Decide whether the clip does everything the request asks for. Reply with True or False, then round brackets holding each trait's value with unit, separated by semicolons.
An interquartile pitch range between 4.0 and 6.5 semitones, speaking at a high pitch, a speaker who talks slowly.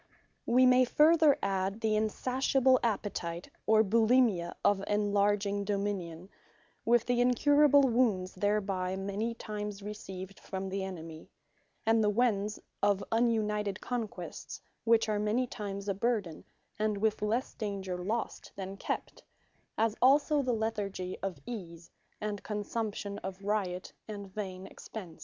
False (2.9 semitones; 210 Hz; 130 wpm)